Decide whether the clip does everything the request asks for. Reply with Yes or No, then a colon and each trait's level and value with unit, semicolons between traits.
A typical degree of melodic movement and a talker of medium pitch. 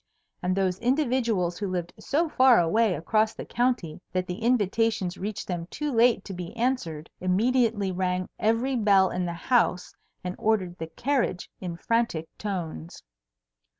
No: average, 4.7 semitones; high, 195 Hz